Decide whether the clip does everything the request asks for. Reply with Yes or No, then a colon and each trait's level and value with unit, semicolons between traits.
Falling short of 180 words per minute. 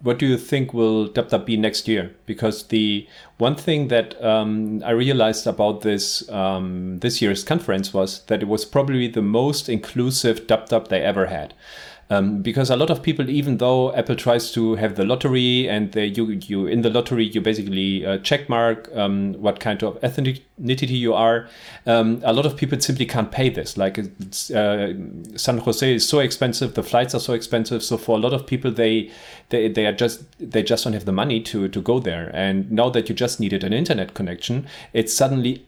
No: fast, 205 wpm